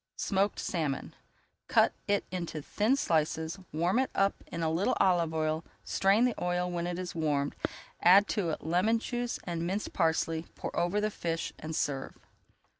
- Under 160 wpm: No, average, 170 wpm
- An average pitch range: Yes, average, 3.6 semitones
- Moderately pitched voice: Yes, medium, 175 Hz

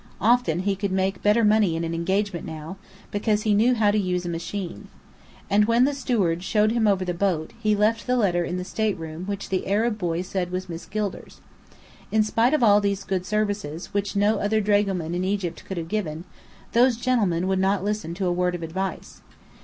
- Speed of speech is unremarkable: No, fast, 210 wpm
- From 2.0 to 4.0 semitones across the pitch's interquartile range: Yes, average, 3.1 semitones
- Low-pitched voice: No, high, 195 Hz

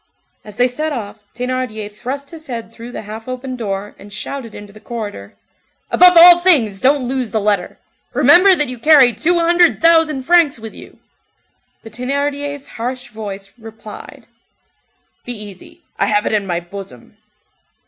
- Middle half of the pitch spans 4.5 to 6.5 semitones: Yes, average, 5.3 semitones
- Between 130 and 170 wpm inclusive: Yes, average, 160 wpm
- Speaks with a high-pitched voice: Yes, high, 245 Hz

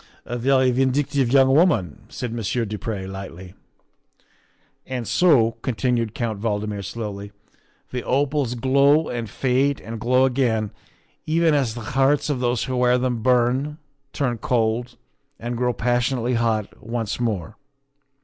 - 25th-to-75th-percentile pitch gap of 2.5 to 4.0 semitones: Yes, average, 2.9 semitones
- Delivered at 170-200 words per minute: No, average, 145 wpm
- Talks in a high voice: No, low, 120 Hz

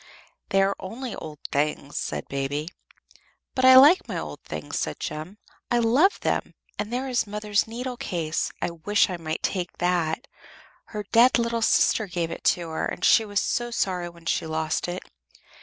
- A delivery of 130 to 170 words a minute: No, average, 180 wpm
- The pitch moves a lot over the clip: Yes, wide, 6.1 semitones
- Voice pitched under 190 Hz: No, high, 195 Hz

